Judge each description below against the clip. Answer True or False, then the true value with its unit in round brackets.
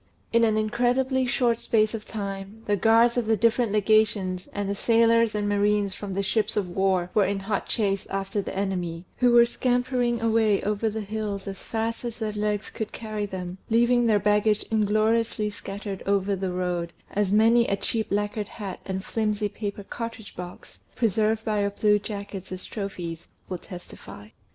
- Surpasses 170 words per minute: True (180 wpm)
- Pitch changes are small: True (2.3 semitones)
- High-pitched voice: True (210 Hz)